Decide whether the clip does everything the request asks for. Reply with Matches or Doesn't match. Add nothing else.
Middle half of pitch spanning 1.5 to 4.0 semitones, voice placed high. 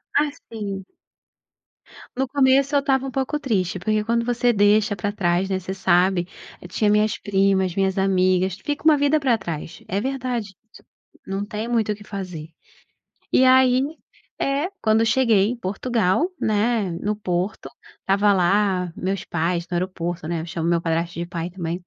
Doesn't match